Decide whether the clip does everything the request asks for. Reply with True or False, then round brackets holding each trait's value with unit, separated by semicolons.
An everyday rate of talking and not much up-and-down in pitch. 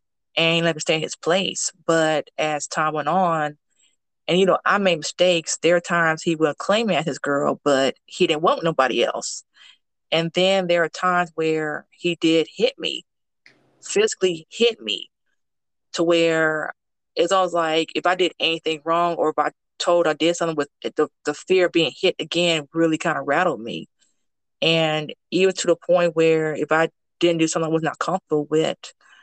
True (195 wpm; 2.0 semitones)